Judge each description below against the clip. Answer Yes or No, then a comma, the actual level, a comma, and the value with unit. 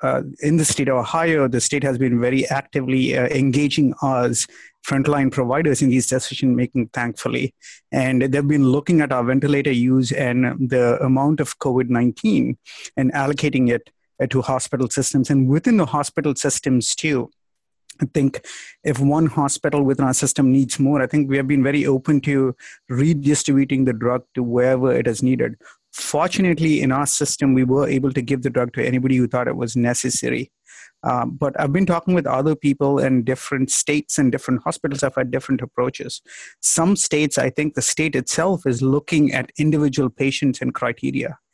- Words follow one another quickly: No, average, 180 wpm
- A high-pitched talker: No, low, 135 Hz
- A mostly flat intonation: Yes, narrow, 2.2 semitones